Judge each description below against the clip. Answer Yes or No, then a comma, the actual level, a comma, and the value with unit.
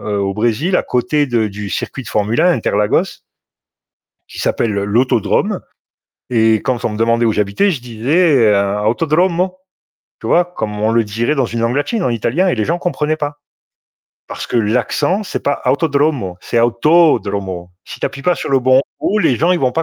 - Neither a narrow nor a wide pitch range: No, wide, 6.4 semitones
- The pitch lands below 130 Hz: Yes, low, 120 Hz